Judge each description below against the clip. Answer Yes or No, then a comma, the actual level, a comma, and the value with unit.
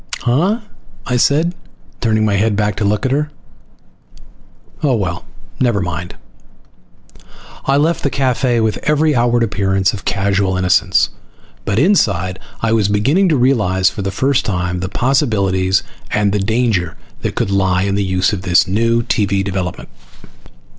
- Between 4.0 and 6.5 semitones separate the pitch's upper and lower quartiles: Yes, average, 4.7 semitones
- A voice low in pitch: Yes, low, 105 Hz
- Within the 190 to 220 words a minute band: No, average, 155 wpm